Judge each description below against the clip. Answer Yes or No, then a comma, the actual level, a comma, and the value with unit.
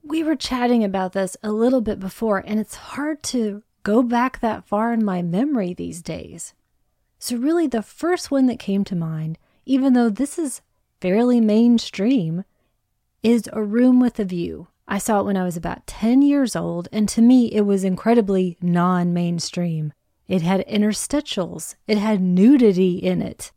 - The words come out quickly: No, average, 175 wpm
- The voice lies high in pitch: Yes, high, 215 Hz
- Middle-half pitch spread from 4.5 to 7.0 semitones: Yes, average, 4.8 semitones